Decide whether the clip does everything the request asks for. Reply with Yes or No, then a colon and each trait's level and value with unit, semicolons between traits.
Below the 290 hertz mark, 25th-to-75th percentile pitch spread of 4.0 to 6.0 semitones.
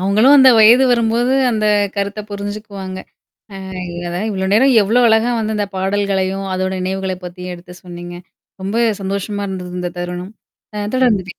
No: high, 200 Hz; average, 2.7 semitones